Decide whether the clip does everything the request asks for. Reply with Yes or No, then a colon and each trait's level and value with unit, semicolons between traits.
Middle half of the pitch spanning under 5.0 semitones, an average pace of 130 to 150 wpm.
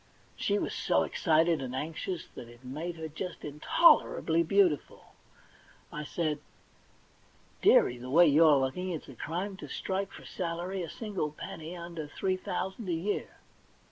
No: average, 3.6 semitones; average, 160 wpm